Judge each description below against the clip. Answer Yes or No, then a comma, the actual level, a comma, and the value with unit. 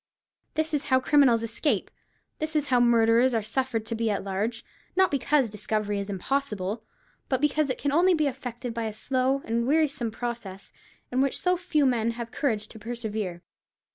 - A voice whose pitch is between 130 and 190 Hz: No, high, 240 Hz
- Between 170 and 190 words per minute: Yes, average, 175 wpm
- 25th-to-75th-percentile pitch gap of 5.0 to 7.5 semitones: No, average, 4.2 semitones